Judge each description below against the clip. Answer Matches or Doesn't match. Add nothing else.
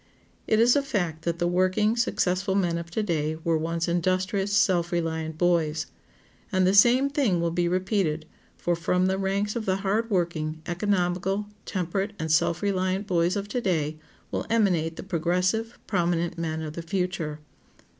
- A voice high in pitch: Doesn't match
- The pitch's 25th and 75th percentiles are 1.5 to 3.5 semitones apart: Matches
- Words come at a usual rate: Matches